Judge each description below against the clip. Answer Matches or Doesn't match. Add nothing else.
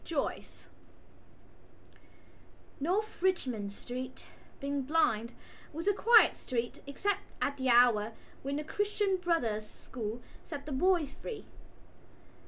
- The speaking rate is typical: Doesn't match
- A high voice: Matches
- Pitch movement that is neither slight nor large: Doesn't match